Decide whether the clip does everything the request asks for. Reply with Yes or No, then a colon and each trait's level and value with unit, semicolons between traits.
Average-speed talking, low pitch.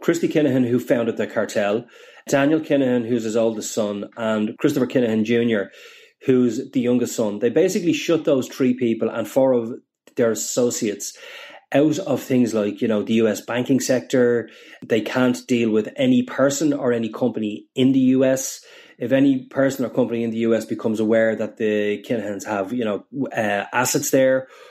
Yes: average, 175 wpm; low, 125 Hz